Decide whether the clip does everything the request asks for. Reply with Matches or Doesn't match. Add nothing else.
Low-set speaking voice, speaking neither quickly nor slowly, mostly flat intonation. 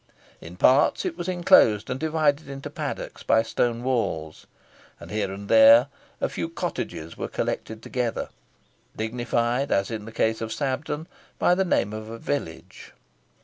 Doesn't match